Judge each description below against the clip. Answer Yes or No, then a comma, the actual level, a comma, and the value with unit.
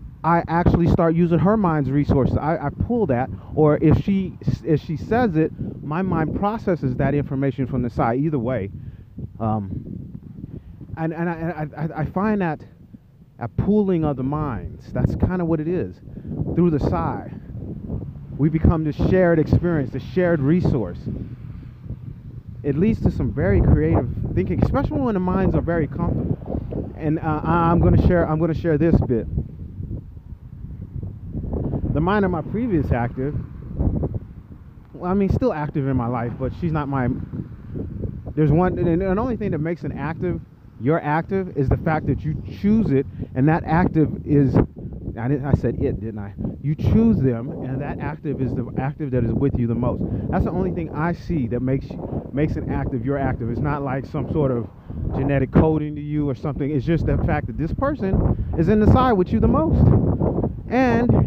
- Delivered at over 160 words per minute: Yes, average, 185 wpm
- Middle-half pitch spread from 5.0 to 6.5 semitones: No, average, 4.5 semitones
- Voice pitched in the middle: Yes, medium, 145 Hz